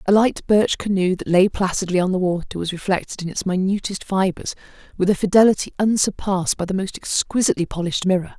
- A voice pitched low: No, high, 190 Hz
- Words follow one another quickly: No, average, 185 wpm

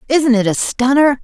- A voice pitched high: Yes, very high, 260 Hz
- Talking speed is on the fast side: No, average, 195 wpm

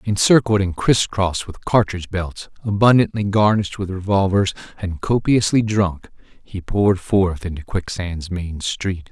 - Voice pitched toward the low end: Yes, very low, 95 Hz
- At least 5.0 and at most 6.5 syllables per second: No, 4.6 syllables/s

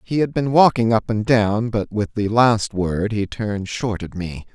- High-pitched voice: No, low, 110 Hz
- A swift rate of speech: Yes, fast, 225 wpm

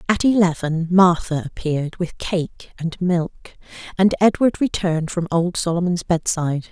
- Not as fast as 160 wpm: Yes, slow, 135 wpm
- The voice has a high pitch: No, medium, 175 Hz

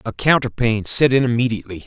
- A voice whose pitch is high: No, low, 120 Hz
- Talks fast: No, average, 195 wpm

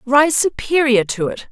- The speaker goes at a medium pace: Yes, average, 160 wpm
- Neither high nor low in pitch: No, very high, 265 Hz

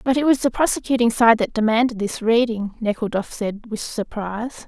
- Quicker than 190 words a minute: No, average, 180 wpm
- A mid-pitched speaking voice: No, high, 230 Hz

